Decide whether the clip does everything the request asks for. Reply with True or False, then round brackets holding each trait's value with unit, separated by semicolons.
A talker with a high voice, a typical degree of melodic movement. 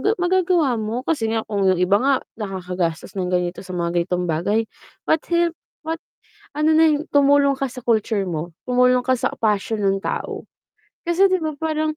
False (235 Hz; 8.5 semitones)